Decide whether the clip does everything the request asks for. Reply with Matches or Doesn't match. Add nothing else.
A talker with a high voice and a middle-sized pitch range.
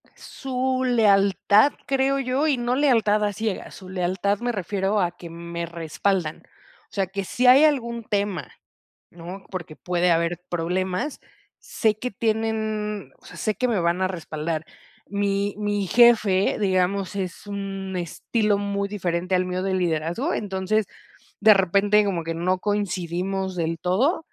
Matches